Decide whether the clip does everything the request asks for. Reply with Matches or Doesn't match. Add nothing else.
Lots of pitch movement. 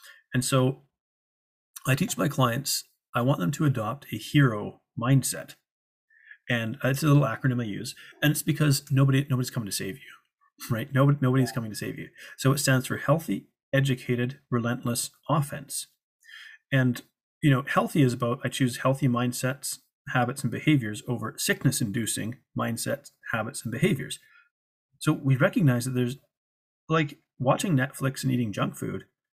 Doesn't match